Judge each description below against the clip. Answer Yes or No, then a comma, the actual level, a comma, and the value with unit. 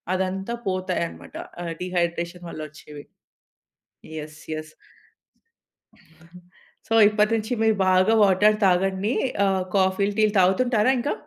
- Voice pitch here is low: No, high, 190 Hz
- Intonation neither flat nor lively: Yes, average, 3.5 semitones